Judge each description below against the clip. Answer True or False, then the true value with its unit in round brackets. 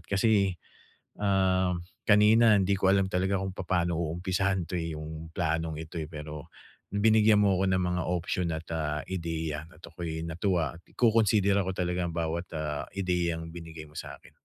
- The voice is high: False (90 Hz)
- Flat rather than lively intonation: False (3.0 semitones)